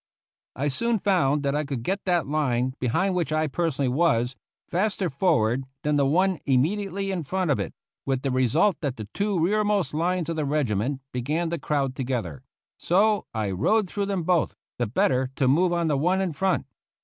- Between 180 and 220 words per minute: Yes, average, 190 wpm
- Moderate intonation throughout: No, wide, 5.8 semitones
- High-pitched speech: No, medium, 155 Hz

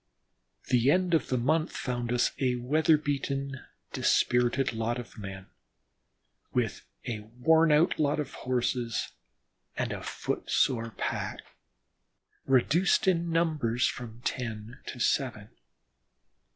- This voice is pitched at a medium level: No, low, 125 Hz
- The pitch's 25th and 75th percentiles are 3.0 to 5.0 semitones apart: Yes, average, 4.1 semitones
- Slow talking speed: Yes, slow, 120 wpm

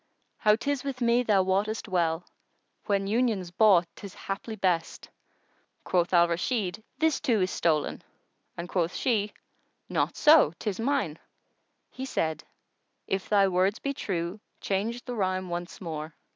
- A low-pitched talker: No, high, 195 Hz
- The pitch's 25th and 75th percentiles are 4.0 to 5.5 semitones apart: Yes, average, 4.6 semitones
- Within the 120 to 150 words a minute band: Yes, average, 145 wpm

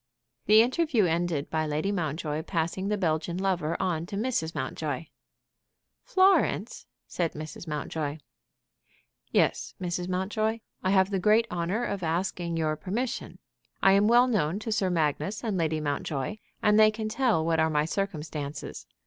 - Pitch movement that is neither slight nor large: Yes, average, 4.9 semitones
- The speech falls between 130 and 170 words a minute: Yes, average, 150 wpm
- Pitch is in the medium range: Yes, medium, 180 Hz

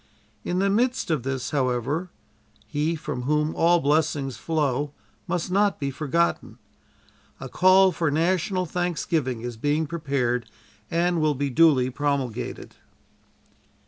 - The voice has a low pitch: No, medium, 150 Hz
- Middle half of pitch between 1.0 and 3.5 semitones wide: No, average, 4.2 semitones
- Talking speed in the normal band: No, slow, 125 wpm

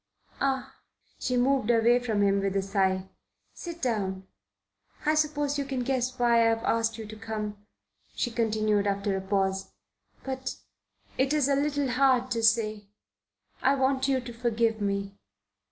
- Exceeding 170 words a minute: No, average, 155 wpm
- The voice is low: No, high, 230 Hz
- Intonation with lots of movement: No, average, 4.2 semitones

